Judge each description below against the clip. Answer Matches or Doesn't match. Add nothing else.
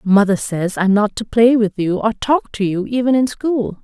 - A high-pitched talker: Matches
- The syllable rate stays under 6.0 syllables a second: Matches